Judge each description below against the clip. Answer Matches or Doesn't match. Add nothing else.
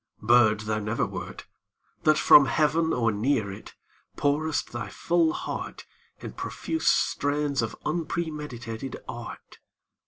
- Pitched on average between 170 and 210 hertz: Doesn't match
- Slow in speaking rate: Matches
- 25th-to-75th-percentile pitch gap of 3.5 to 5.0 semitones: Doesn't match